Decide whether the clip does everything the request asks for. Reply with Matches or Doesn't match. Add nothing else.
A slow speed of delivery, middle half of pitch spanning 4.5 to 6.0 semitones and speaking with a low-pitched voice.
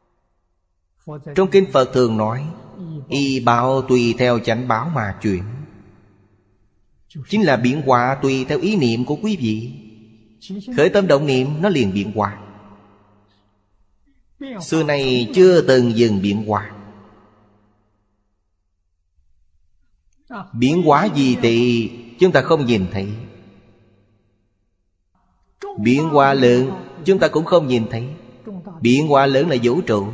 Matches